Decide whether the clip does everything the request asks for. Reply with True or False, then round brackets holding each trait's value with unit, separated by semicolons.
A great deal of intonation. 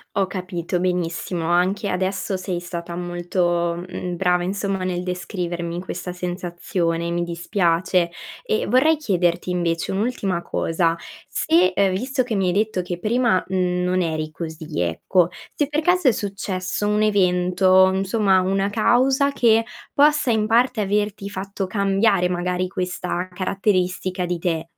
False (2.5 semitones)